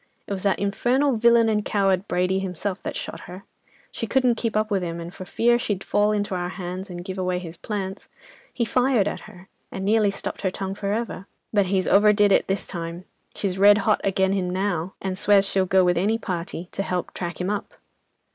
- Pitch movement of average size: No, narrow, 2.3 semitones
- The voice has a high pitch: Yes, high, 195 Hz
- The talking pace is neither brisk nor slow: No, fast, 215 wpm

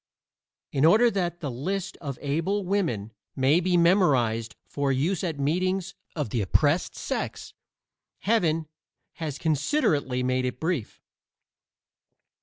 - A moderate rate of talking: No, slow, 120 wpm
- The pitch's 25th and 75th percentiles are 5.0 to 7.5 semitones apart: Yes, wide, 5.5 semitones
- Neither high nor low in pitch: Yes, medium, 155 Hz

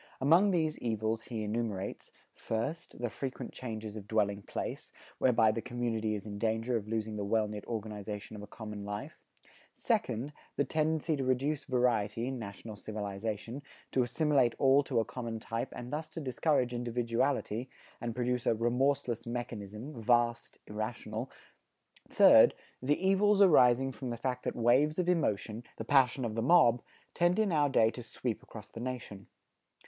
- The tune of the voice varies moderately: Yes, average, 3.4 semitones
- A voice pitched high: No, low, 120 Hz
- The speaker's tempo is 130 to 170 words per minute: Yes, average, 165 wpm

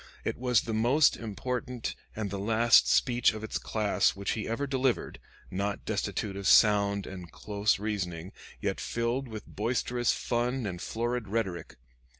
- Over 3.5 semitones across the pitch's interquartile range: No, average, 3.2 semitones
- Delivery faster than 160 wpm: No, average, 155 wpm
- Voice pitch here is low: Yes, low, 110 Hz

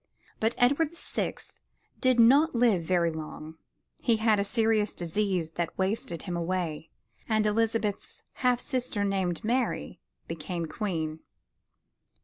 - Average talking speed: No, slow, 125 wpm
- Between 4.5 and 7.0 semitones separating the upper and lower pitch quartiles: Yes, average, 5.2 semitones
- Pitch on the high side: Yes, high, 205 Hz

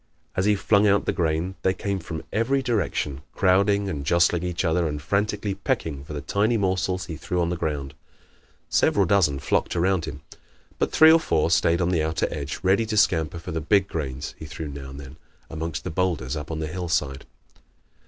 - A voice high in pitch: No, very low, 85 Hz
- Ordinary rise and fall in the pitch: Yes, average, 4.2 semitones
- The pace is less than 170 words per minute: No, fast, 205 wpm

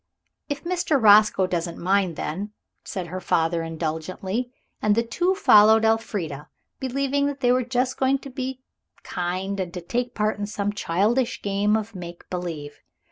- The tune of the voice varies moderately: No, wide, 5.8 semitones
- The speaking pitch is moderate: No, high, 205 Hz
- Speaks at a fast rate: No, average, 160 wpm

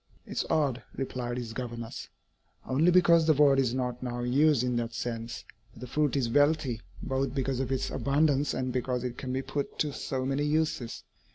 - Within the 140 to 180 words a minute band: No, average, 195 wpm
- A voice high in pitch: No, low, 130 Hz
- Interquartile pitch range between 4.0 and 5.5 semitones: No, average, 2.9 semitones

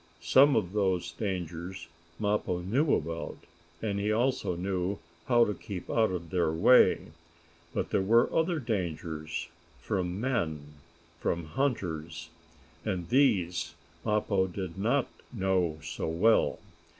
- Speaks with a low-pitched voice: Yes, very low, 95 Hz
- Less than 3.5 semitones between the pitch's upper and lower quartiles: No, average, 4.6 semitones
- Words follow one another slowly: Yes, slow, 125 wpm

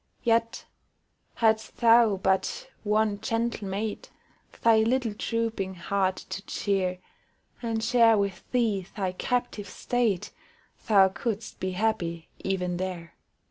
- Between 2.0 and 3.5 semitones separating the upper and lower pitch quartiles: Yes, average, 3.2 semitones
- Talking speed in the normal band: No, slow, 115 wpm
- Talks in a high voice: Yes, high, 210 Hz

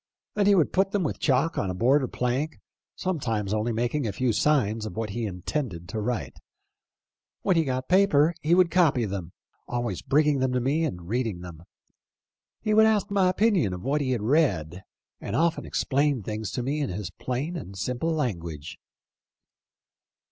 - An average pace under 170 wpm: No, average, 185 wpm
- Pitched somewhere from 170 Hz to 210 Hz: No, low, 130 Hz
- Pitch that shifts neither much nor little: No, wide, 6.9 semitones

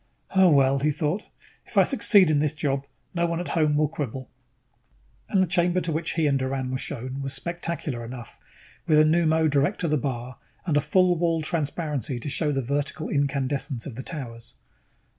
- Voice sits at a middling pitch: Yes, medium, 150 Hz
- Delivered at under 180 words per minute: No, average, 195 wpm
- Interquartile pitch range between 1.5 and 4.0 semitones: Yes, average, 3.6 semitones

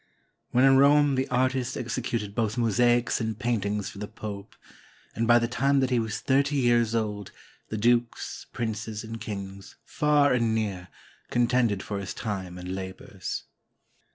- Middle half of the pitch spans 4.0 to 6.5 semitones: No, average, 3.2 semitones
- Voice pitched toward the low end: Yes, low, 115 Hz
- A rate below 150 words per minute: No, average, 160 wpm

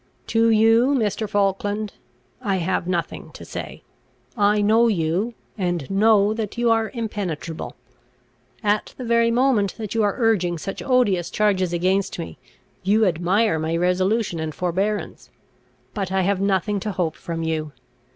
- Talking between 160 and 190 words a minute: No, average, 150 wpm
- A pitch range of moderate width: Yes, average, 3.7 semitones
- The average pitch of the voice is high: Yes, high, 200 Hz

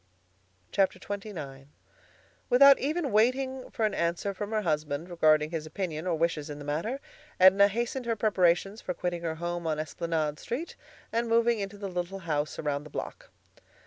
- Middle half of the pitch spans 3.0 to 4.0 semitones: No, wide, 5.6 semitones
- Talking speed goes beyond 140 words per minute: Yes, average, 165 wpm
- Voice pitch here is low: No, medium, 180 Hz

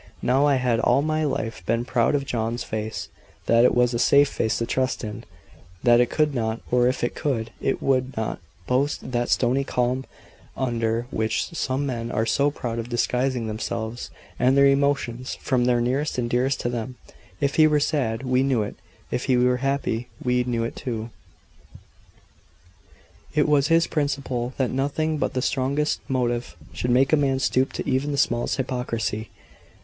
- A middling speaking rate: Yes, average, 180 wpm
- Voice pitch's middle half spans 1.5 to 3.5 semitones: Yes, narrow, 2.6 semitones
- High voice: No, low, 125 Hz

